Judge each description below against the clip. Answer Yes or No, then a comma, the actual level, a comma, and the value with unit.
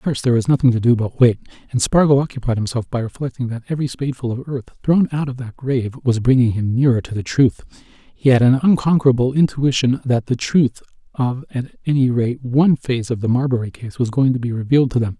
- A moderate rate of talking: No, fast, 225 wpm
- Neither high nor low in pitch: No, low, 125 Hz